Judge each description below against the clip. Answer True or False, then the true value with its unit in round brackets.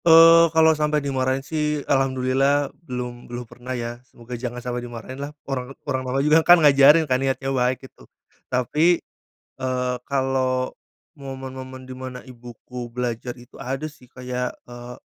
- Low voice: True (130 Hz)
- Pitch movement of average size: False (2.1 semitones)